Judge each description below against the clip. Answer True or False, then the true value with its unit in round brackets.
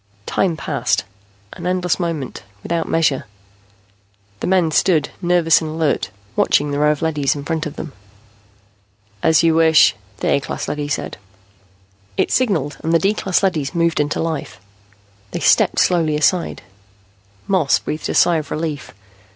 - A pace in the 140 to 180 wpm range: True (155 wpm)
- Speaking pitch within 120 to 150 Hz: False (160 Hz)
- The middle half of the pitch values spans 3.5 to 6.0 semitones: False (2.6 semitones)